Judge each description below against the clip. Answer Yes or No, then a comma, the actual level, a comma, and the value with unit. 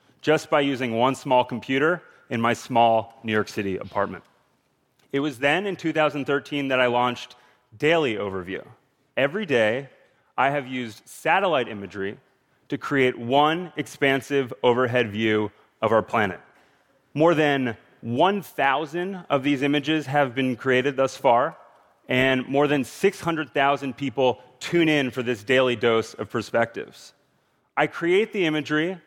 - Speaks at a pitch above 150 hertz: No, low, 135 Hz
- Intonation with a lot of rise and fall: No, average, 3.3 semitones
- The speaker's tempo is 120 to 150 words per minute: Yes, fast, 140 wpm